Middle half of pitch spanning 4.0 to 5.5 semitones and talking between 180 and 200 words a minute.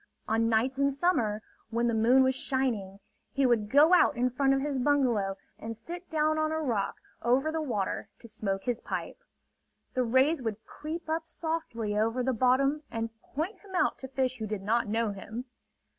Yes: average, 4.5 semitones; average, 190 wpm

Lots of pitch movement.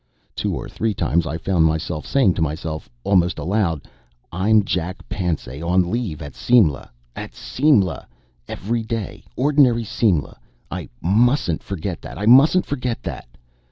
Yes: wide, 6.1 semitones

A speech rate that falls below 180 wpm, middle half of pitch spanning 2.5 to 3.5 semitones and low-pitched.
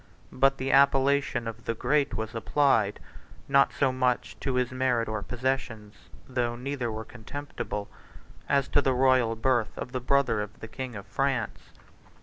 Yes: average, 160 wpm; average, 3.1 semitones; low, 125 Hz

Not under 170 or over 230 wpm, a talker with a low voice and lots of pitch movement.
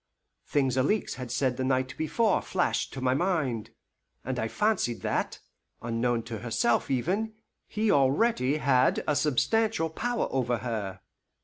No: average, 140 wpm; low, 130 Hz; wide, 6.5 semitones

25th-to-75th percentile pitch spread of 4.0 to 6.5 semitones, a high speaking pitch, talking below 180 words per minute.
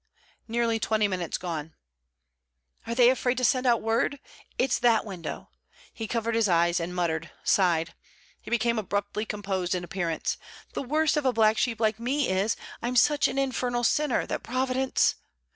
Yes: average, 4.9 semitones; high, 225 Hz; average, 165 wpm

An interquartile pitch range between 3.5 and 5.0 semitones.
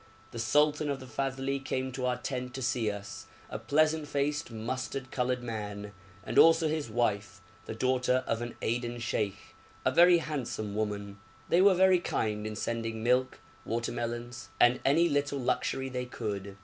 Yes: average, 4.0 semitones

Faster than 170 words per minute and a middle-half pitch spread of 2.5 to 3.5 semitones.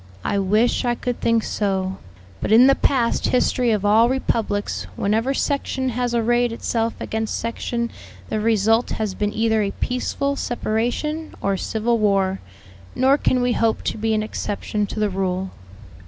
No: average, 160 wpm; average, 2.8 semitones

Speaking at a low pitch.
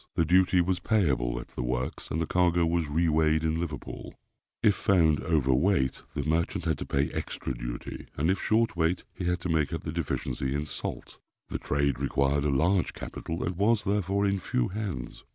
Yes: very low, 80 Hz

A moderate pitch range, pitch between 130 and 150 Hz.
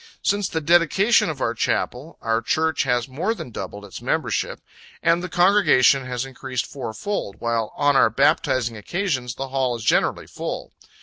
No: wide, 5.9 semitones; low, 135 Hz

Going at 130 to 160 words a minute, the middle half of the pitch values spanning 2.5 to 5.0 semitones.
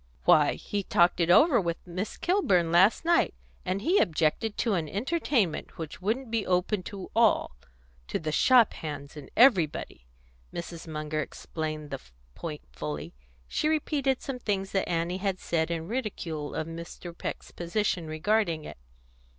No: average, 155 wpm; wide, 5.6 semitones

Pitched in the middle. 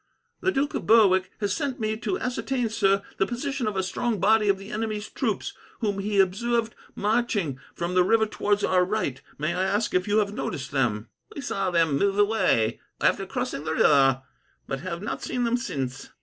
No: high, 205 Hz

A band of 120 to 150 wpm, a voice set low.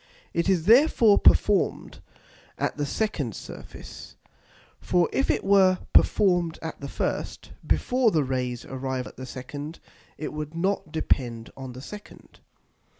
No: average, 140 wpm; medium, 160 Hz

